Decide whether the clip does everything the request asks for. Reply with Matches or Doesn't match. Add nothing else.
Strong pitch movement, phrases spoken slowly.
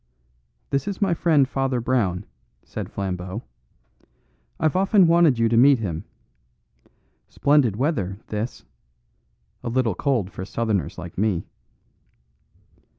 Matches